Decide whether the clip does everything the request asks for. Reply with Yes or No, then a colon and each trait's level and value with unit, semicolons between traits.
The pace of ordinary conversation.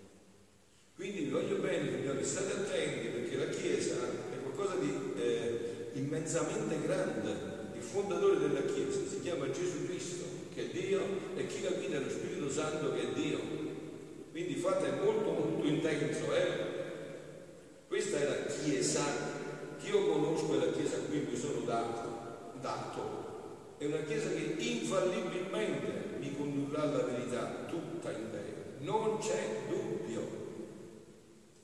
Yes: average, 140 wpm